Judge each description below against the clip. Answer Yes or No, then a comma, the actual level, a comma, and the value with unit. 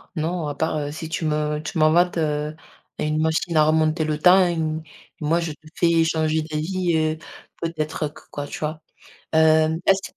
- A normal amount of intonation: No, narrow, 1.4 semitones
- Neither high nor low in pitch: Yes, medium, 155 Hz